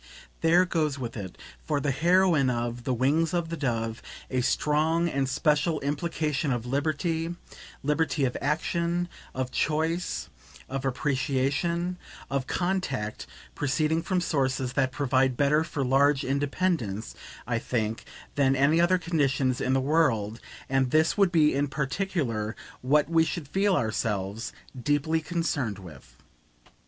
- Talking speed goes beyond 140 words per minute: No, slow, 135 wpm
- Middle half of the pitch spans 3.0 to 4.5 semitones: Yes, average, 4.1 semitones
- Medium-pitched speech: Yes, medium, 145 Hz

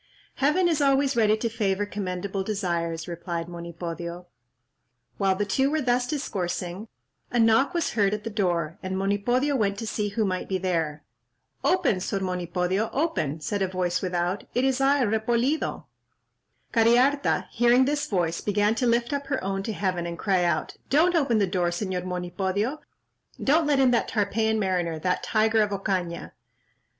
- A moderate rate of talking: Yes, average, 160 wpm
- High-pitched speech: Yes, high, 205 Hz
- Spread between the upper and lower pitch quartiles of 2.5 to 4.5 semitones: No, average, 5.2 semitones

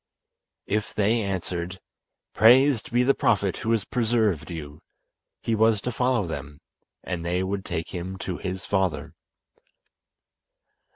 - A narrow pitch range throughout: No, average, 4.2 semitones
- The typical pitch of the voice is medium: No, low, 100 Hz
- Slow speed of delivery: Yes, slow, 130 wpm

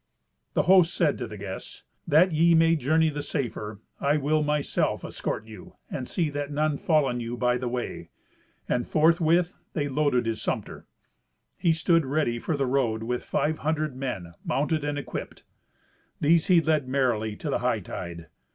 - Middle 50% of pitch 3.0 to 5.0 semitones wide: Yes, average, 4.4 semitones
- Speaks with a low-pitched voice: No, medium, 145 Hz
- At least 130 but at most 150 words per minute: No, average, 170 wpm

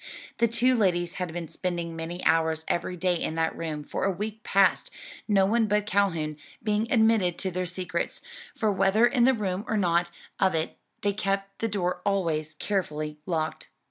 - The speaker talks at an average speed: Yes, average, 180 wpm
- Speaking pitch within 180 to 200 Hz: Yes, medium, 185 Hz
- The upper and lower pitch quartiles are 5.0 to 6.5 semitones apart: No, average, 3.7 semitones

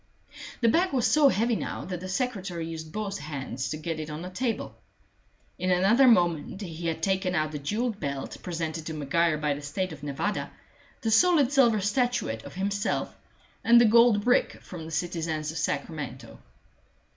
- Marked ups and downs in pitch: Yes, wide, 6.0 semitones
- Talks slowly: No, average, 180 wpm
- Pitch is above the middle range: No, medium, 180 Hz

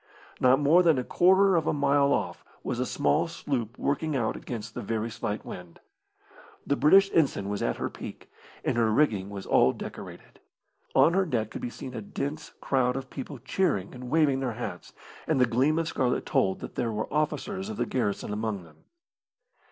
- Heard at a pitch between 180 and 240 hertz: No, low, 130 Hz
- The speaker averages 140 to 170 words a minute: No, average, 195 wpm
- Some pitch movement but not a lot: No, wide, 5.7 semitones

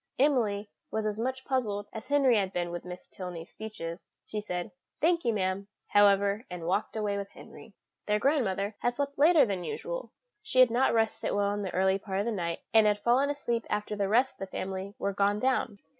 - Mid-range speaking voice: No, high, 210 Hz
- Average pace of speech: No, fast, 210 wpm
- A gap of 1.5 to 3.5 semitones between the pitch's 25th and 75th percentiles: No, average, 4.0 semitones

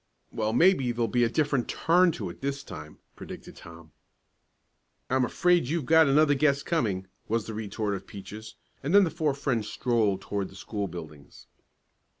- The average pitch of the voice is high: No, low, 120 Hz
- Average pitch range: No, wide, 6.5 semitones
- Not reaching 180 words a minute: Yes, average, 170 wpm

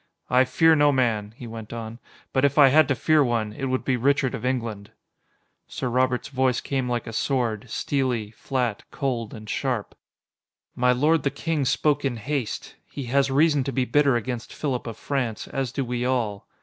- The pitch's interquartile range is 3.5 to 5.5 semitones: No, average, 2.9 semitones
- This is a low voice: Yes, low, 130 Hz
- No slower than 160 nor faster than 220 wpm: Yes, average, 190 wpm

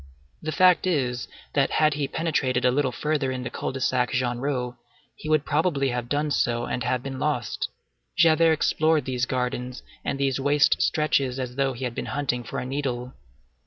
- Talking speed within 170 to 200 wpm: Yes, average, 190 wpm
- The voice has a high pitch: No, low, 135 Hz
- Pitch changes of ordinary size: Yes, average, 3.1 semitones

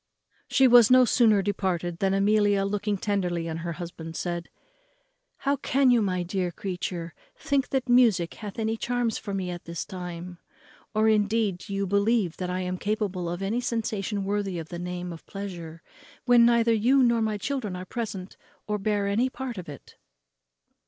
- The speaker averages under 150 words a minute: No, average, 175 wpm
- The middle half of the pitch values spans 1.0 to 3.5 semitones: No, average, 4.1 semitones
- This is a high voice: Yes, high, 200 Hz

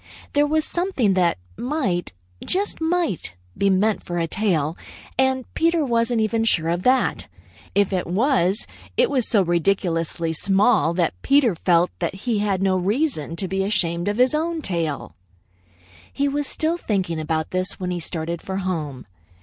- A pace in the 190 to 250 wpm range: No, average, 165 wpm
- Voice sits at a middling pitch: No, high, 195 Hz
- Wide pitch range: Yes, wide, 7.0 semitones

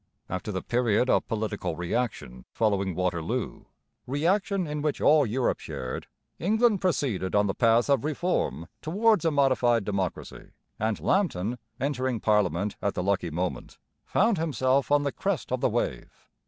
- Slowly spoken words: No, average, 150 wpm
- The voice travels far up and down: Yes, wide, 7.1 semitones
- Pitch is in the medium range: No, low, 120 Hz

